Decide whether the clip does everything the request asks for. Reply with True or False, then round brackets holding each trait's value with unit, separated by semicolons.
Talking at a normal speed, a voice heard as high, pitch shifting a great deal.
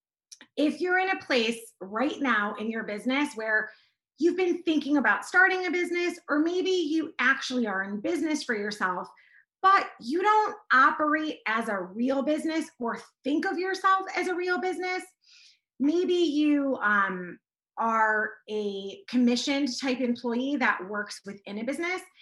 True (150 wpm; 280 Hz; 8.1 semitones)